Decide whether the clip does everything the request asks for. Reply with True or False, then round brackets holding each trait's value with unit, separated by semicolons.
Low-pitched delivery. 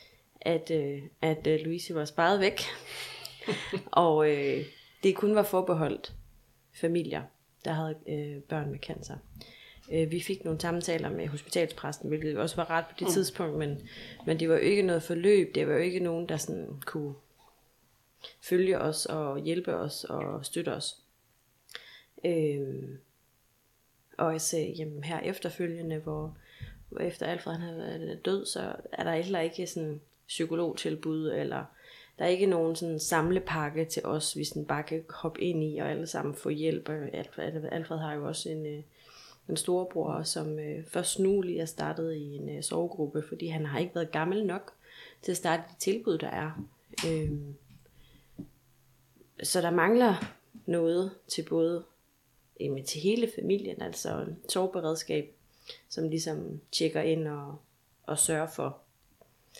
False (160 Hz)